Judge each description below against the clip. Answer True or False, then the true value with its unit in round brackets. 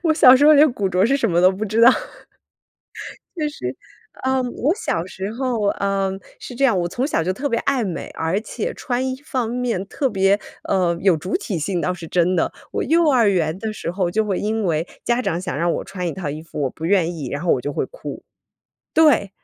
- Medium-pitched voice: False (195 Hz)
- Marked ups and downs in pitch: True (6.1 semitones)